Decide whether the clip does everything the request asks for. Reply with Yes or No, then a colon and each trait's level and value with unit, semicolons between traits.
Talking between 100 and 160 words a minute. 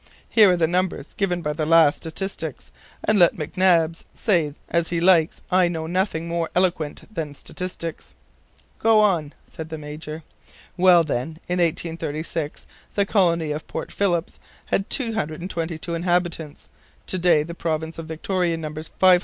Yes: average, 150 wpm